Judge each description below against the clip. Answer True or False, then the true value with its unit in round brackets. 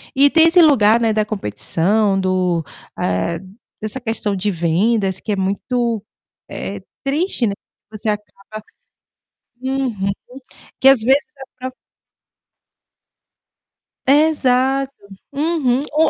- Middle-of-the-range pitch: False (230 Hz)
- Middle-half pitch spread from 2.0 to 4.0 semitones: False (5.4 semitones)